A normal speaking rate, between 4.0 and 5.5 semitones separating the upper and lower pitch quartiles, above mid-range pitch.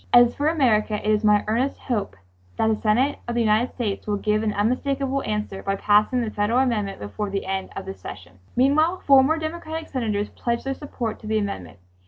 No: fast, 210 wpm; average, 4.3 semitones; high, 220 Hz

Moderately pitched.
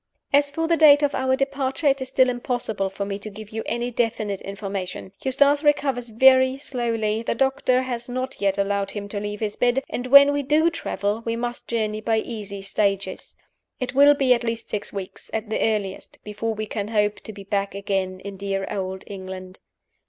No: high, 225 Hz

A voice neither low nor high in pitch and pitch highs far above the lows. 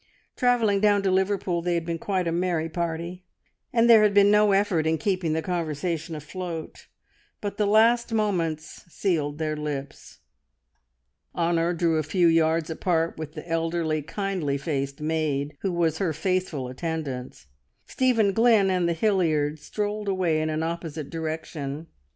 No: medium, 170 Hz; average, 3.8 semitones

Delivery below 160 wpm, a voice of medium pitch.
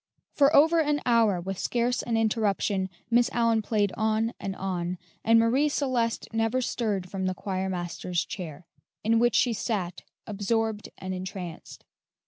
No: average, 145 wpm; high, 220 Hz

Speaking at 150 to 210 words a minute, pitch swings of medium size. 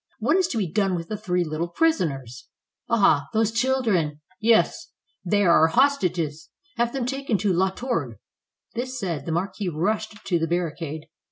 No: average, 170 wpm; wide, 5.8 semitones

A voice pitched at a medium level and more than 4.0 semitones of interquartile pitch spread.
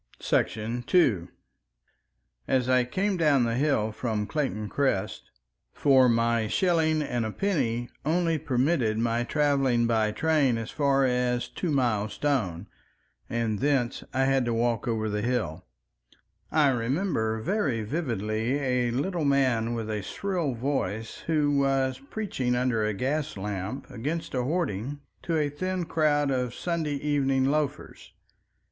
No: low, 130 Hz; average, 4.5 semitones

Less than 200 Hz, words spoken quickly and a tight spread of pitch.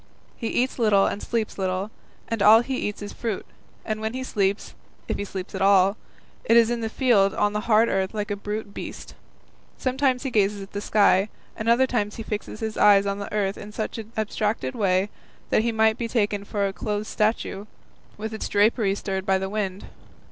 No: high, 210 Hz; fast, 210 wpm; narrow, 2.0 semitones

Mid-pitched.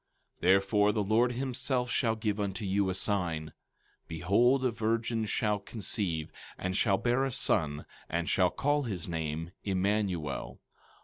No: low, 100 Hz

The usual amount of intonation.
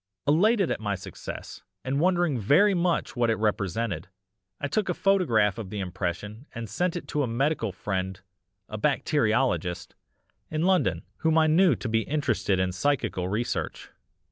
No: wide, 7.5 semitones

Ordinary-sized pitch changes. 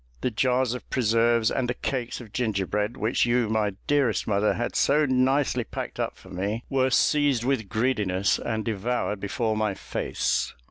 Yes: average, 3.1 semitones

